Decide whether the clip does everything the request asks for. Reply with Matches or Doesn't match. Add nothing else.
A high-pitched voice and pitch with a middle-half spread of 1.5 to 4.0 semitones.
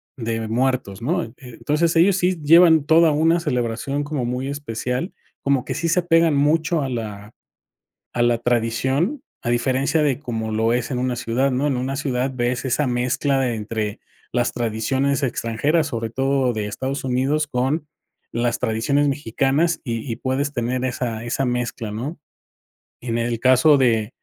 Doesn't match